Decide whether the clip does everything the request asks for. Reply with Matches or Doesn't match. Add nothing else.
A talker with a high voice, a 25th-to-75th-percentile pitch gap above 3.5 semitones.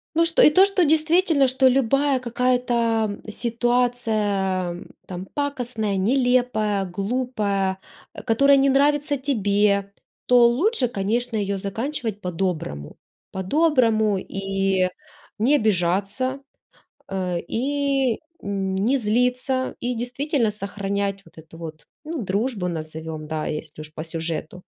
Matches